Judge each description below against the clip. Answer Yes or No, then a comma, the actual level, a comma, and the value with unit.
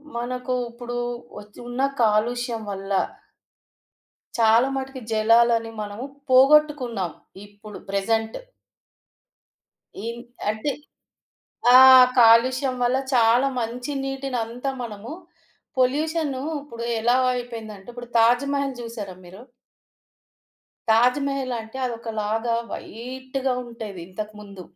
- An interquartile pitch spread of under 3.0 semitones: Yes, narrow, 2.6 semitones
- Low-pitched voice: No, high, 235 Hz